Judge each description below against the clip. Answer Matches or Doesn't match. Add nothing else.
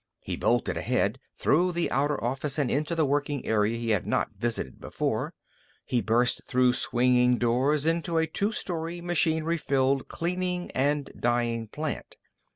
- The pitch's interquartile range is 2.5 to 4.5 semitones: Doesn't match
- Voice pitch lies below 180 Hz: Matches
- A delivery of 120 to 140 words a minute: Doesn't match